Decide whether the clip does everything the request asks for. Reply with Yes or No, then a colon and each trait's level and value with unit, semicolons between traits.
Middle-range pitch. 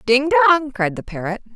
No: very high, 250 Hz